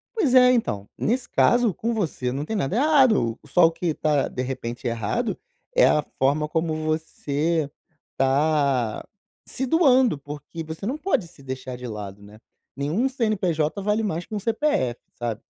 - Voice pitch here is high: No, medium, 155 Hz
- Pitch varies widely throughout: Yes, wide, 8.9 semitones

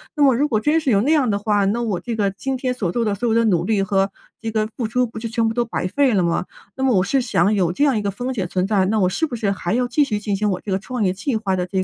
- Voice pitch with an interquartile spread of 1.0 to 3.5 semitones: No, average, 4.1 semitones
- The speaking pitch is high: Yes, high, 215 Hz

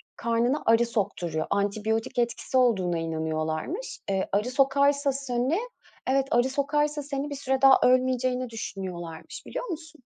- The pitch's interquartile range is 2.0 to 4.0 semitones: No, wide, 5.4 semitones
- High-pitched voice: Yes, very high, 250 Hz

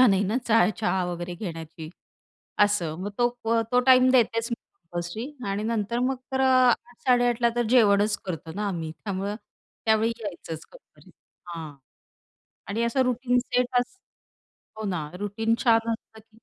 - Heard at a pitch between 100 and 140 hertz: No, high, 220 Hz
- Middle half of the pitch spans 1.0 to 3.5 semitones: No, average, 4.4 semitones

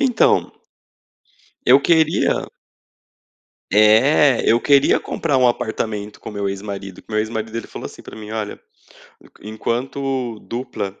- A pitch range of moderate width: Yes, average, 4.1 semitones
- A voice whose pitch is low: Yes, low, 115 Hz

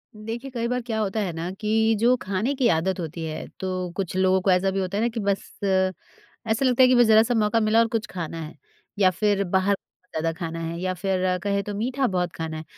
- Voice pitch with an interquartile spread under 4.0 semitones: Yes, average, 3.4 semitones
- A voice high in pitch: Yes, high, 195 Hz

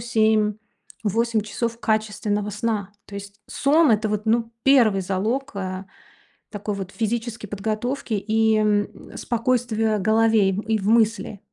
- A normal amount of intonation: No, narrow, 1.9 semitones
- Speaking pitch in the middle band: No, high, 215 Hz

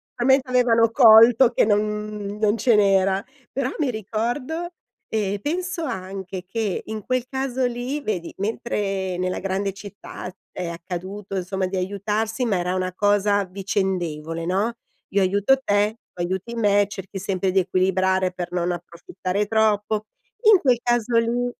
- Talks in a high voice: Yes, high, 205 Hz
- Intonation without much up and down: No, average, 3.5 semitones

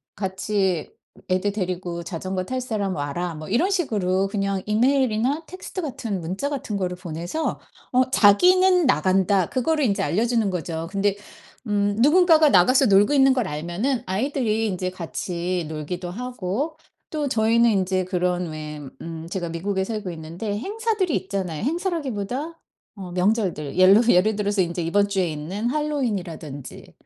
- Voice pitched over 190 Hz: Yes, high, 200 Hz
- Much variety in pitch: Yes, wide, 5.9 semitones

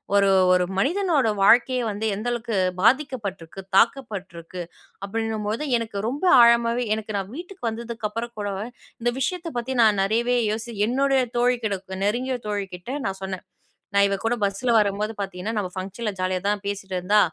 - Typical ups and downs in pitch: Yes, average, 3.5 semitones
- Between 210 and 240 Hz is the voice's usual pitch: Yes, high, 220 Hz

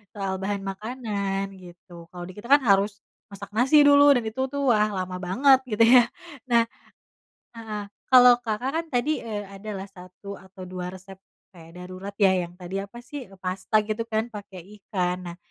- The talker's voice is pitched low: No, high, 200 Hz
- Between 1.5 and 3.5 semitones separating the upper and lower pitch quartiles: No, average, 4.1 semitones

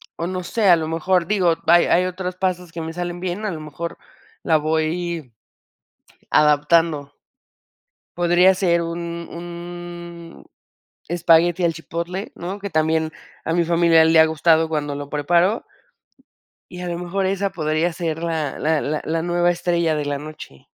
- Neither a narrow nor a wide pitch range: No, narrow, 1.7 semitones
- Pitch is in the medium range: Yes, medium, 170 Hz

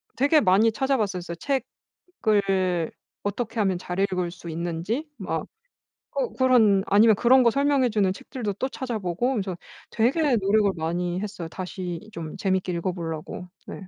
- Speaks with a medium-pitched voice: No, high, 200 Hz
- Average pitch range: Yes, average, 4.8 semitones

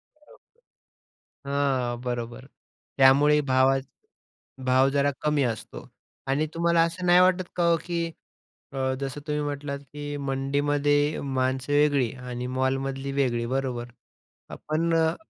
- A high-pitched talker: No, medium, 140 Hz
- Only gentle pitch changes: Yes, narrow, 2.2 semitones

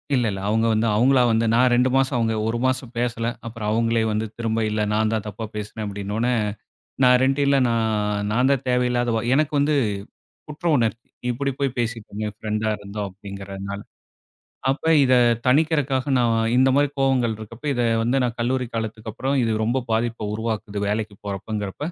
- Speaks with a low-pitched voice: Yes, low, 115 Hz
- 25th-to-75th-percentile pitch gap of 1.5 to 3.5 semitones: Yes, average, 2.9 semitones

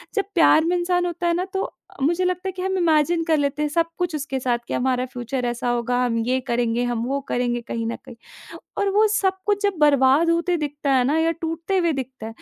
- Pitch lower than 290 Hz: No, very high, 300 Hz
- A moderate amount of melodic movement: No, wide, 6.0 semitones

